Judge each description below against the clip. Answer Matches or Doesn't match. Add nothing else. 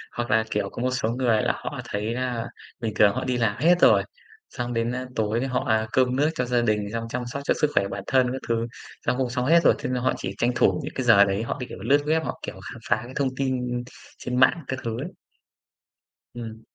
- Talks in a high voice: Doesn't match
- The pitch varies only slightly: Matches